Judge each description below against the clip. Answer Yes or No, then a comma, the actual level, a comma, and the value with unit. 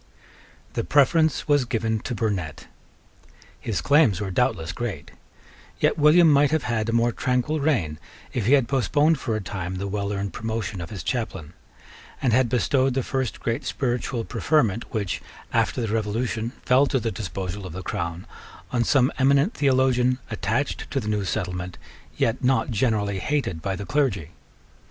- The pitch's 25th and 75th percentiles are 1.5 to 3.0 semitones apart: No, average, 5.0 semitones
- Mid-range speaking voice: No, low, 115 Hz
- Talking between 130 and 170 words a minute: Yes, average, 165 wpm